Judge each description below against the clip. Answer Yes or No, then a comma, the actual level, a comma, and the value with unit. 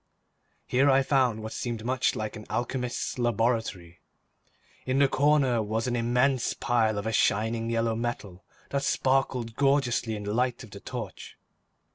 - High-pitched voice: No, low, 120 Hz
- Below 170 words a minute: Yes, average, 155 wpm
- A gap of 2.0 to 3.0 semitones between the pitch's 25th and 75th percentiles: Yes, average, 2.7 semitones